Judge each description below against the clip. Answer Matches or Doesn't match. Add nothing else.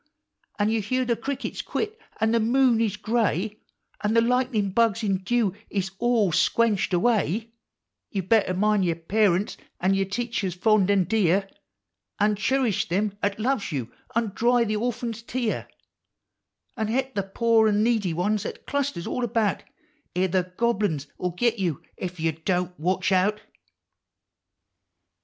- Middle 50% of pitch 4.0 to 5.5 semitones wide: Doesn't match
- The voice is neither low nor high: Doesn't match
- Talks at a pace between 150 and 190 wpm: Matches